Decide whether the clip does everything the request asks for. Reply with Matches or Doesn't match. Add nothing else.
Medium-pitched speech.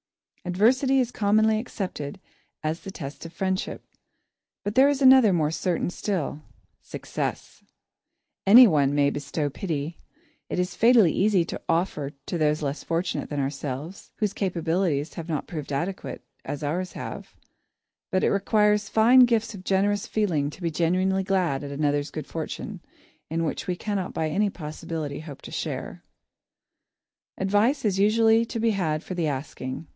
Matches